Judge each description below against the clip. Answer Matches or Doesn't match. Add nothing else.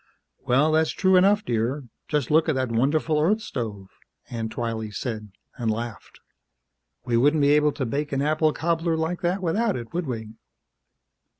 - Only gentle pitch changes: Doesn't match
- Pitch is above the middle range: Doesn't match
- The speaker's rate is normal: Matches